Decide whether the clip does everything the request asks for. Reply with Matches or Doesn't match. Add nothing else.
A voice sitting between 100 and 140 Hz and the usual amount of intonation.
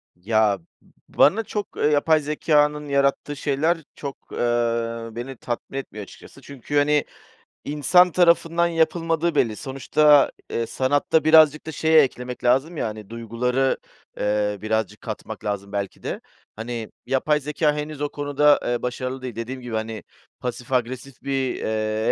Matches